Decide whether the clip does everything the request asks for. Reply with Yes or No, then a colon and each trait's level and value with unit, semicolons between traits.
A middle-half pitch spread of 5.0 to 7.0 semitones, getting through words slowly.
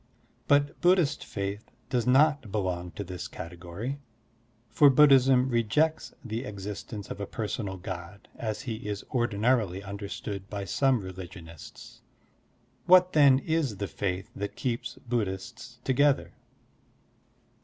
Yes: wide, 5.4 semitones; slow, 125 wpm